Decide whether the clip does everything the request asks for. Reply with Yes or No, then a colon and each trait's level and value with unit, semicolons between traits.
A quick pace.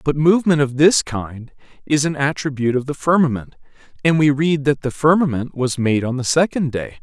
No: average, 195 wpm